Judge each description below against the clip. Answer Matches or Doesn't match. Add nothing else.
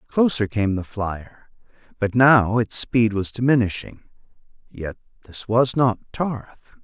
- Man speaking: Matches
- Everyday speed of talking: Doesn't match